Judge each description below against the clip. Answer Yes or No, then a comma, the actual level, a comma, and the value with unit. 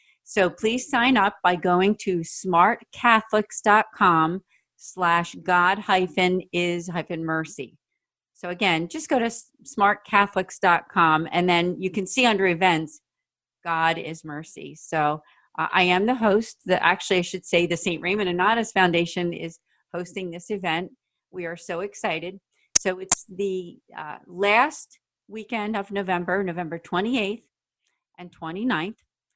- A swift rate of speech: No, slow, 135 wpm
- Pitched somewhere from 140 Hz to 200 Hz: Yes, medium, 185 Hz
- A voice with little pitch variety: No, average, 3.1 semitones